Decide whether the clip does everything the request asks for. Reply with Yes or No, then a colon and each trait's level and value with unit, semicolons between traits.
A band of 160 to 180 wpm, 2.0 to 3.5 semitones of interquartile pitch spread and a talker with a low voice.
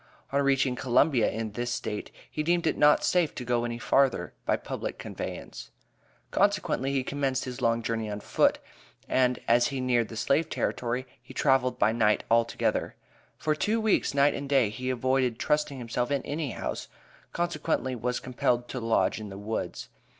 Yes: average, 175 wpm; average, 3.1 semitones; low, 125 Hz